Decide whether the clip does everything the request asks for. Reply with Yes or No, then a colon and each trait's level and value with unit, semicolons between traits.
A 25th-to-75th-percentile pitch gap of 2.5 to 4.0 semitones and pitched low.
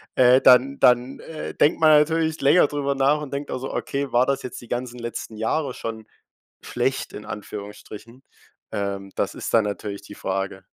No: average, 4.6 semitones; low, 125 Hz